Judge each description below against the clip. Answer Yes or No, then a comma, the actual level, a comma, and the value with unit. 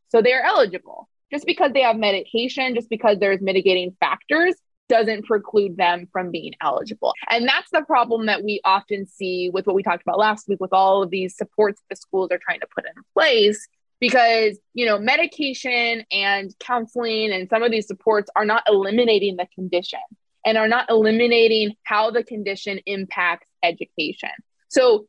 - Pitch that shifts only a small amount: No, average, 3.5 semitones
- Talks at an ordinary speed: Yes, average, 175 wpm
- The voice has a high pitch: Yes, high, 215 Hz